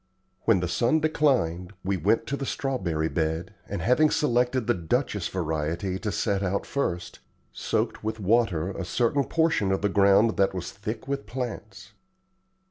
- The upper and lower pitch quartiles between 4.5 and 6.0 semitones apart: Yes, average, 5.3 semitones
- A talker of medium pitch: No, low, 100 Hz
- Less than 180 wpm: Yes, average, 160 wpm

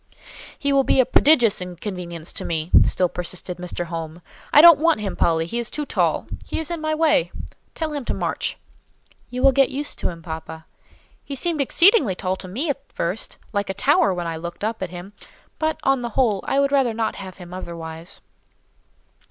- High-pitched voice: Yes, high, 205 Hz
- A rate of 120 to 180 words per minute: No, average, 200 wpm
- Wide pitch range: Yes, wide, 8.0 semitones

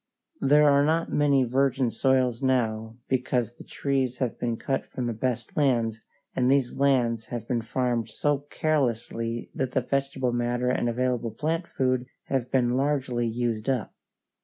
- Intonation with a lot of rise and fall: No, narrow, 2.4 semitones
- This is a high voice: No, low, 125 Hz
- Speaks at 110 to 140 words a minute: No, average, 160 wpm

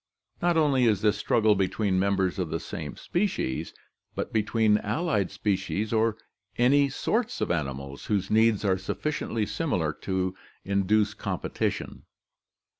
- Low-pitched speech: Yes, low, 105 Hz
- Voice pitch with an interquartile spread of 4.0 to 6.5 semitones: No, average, 3.4 semitones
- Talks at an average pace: No, slow, 130 wpm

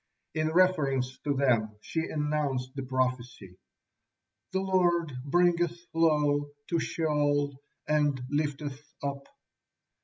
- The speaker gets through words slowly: Yes, slow, 100 wpm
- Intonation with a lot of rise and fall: No, average, 3.2 semitones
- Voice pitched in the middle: Yes, medium, 145 Hz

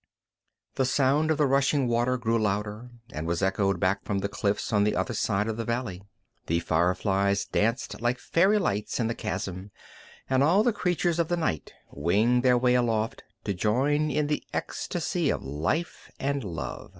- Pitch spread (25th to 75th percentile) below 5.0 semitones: No, wide, 5.5 semitones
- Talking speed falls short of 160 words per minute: No, average, 180 wpm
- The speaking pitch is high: No, low, 115 Hz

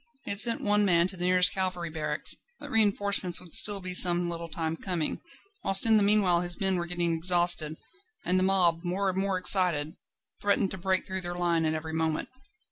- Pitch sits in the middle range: Yes, medium, 180 Hz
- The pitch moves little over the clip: Yes, narrow, 2.2 semitones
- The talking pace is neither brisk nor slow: No, fast, 210 wpm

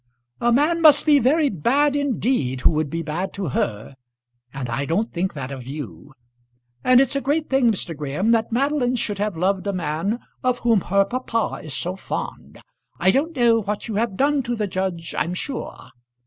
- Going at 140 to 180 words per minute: No, average, 195 wpm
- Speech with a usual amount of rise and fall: No, wide, 7.6 semitones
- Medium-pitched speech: No, high, 205 Hz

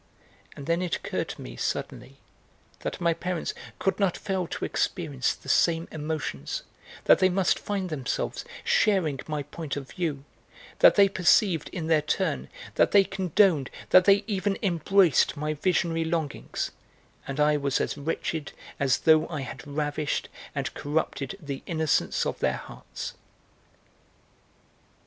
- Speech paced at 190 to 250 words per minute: No, average, 145 wpm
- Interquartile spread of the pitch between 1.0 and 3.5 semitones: No, average, 4.0 semitones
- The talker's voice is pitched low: No, medium, 160 Hz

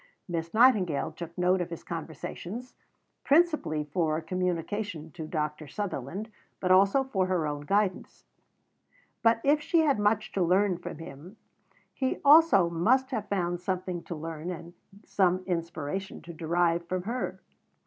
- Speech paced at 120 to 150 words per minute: Yes, average, 145 wpm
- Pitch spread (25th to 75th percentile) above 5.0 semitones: No, average, 3.9 semitones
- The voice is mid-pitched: Yes, medium, 180 Hz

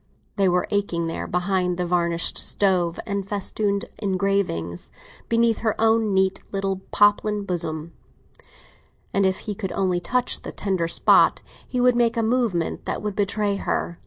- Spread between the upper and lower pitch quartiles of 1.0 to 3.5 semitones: Yes, average, 2.9 semitones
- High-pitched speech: Yes, high, 195 Hz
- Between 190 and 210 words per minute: No, average, 155 wpm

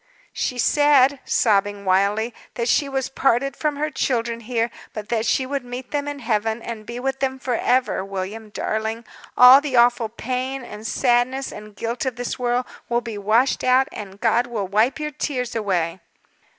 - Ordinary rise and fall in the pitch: Yes, average, 3.2 semitones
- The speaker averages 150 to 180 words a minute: Yes, average, 175 wpm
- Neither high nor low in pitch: No, high, 240 Hz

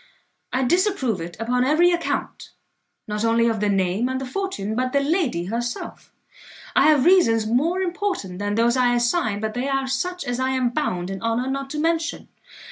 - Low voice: No, very high, 250 Hz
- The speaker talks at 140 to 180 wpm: No, average, 190 wpm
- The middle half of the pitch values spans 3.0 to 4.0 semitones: No, wide, 5.4 semitones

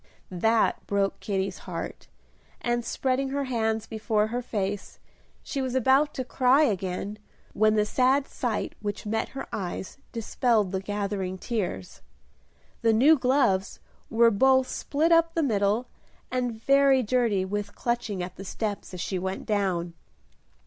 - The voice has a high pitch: Yes, high, 220 Hz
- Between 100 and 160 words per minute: Yes, average, 145 wpm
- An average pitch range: Yes, average, 4.3 semitones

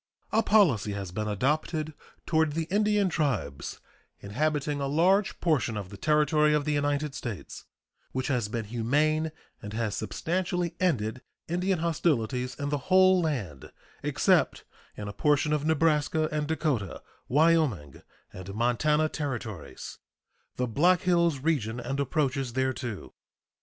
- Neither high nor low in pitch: Yes, medium, 145 Hz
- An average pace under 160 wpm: Yes, slow, 135 wpm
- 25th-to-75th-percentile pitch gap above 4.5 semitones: Yes, average, 5.3 semitones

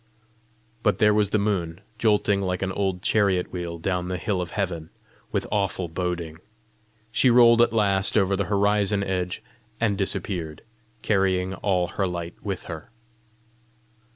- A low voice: Yes, very low, 95 Hz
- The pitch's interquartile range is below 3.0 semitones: Yes, narrow, 2.5 semitones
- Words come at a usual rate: Yes, average, 150 wpm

